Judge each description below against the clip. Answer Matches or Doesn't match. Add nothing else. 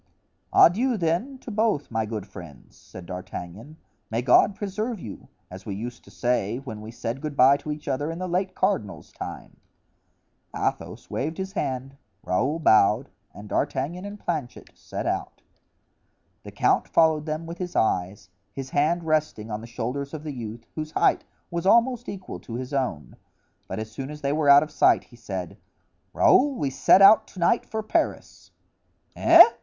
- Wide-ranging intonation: Matches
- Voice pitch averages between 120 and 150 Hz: Matches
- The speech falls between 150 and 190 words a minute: Matches